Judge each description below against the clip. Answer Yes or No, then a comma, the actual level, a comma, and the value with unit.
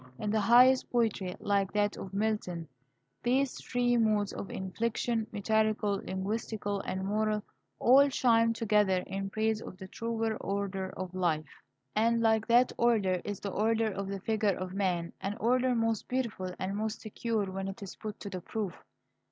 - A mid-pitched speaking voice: No, high, 210 Hz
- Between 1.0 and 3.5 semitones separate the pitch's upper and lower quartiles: Yes, average, 2.7 semitones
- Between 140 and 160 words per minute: No, average, 170 wpm